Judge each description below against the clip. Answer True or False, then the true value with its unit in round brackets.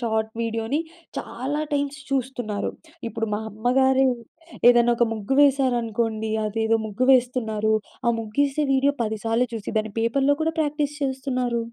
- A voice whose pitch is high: True (240 Hz)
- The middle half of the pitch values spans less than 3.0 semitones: False (3.3 semitones)